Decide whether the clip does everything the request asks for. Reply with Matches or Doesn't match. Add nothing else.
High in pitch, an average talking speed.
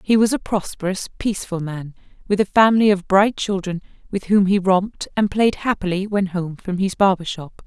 Matches